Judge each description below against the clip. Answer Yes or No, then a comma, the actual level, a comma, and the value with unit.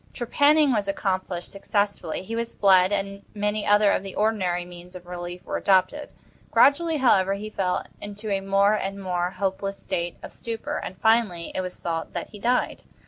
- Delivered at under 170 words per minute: No, average, 180 wpm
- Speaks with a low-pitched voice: No, high, 195 Hz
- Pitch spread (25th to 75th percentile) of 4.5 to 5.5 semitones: No, average, 2.7 semitones